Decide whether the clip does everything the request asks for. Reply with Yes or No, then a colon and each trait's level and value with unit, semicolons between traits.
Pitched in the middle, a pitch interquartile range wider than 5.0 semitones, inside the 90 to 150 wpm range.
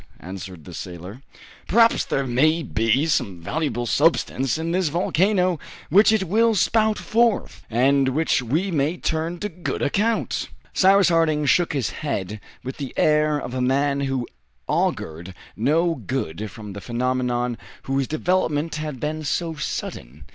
Yes: medium, 145 Hz; wide, 5.6 semitones; average, 145 wpm